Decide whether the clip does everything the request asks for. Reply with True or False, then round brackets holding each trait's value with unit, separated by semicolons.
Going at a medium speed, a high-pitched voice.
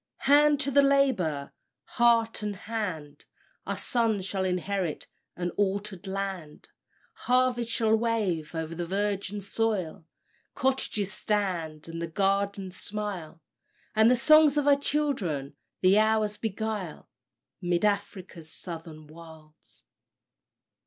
False (110 wpm; 200 Hz)